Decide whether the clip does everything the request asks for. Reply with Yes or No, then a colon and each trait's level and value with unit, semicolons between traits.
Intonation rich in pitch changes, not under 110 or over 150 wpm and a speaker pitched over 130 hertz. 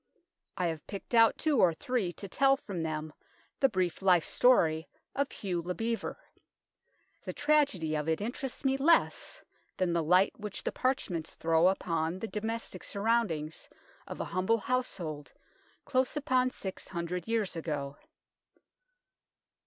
Yes: wide, 6.9 semitones; average, 145 wpm; high, 190 Hz